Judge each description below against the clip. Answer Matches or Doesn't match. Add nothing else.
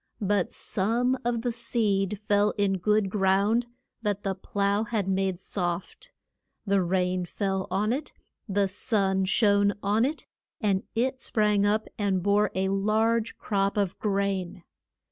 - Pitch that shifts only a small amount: Matches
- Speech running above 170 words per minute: Doesn't match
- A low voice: Doesn't match